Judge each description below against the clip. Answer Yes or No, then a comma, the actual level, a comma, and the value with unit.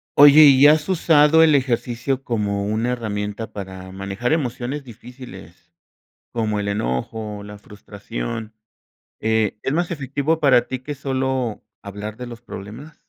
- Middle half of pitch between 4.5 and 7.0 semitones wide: Yes, average, 5.0 semitones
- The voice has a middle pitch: No, low, 120 Hz